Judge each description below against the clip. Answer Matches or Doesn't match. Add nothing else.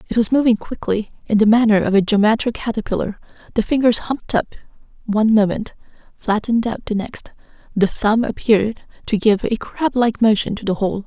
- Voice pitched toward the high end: Matches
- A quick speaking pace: Doesn't match